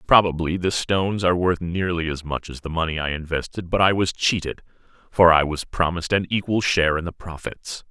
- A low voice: Yes, very low, 85 Hz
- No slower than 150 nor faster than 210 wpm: Yes, fast, 205 wpm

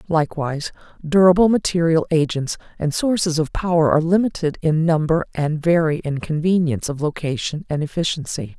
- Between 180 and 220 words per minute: No, average, 140 wpm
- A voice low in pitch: No, medium, 160 Hz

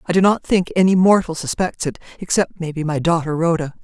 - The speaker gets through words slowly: No, fast, 205 wpm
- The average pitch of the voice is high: No, medium, 170 Hz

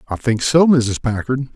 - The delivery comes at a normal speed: Yes, average, 195 wpm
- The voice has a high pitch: No, low, 125 Hz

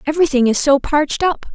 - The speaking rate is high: No, average, 195 wpm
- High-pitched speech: Yes, very high, 295 Hz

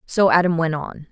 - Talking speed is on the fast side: Yes, fast, 215 wpm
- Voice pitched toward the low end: No, medium, 165 Hz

